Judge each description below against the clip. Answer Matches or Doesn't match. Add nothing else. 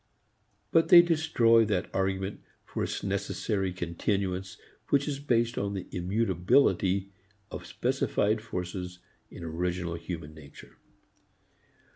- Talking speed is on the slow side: Matches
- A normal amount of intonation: Matches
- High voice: Doesn't match